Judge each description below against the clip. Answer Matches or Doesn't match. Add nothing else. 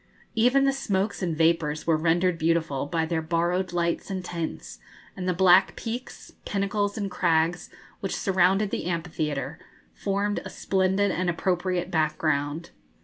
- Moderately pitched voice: Matches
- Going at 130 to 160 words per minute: Matches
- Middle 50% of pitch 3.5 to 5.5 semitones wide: Doesn't match